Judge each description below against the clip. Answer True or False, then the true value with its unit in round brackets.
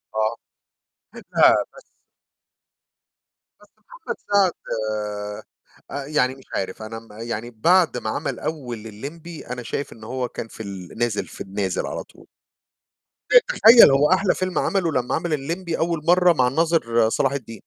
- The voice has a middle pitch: False (130 Hz)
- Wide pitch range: True (7.1 semitones)